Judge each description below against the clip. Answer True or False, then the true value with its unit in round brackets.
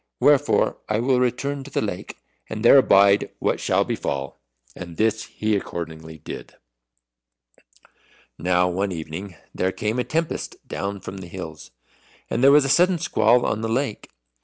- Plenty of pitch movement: True (5.8 semitones)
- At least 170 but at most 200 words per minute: False (160 wpm)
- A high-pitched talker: False (105 Hz)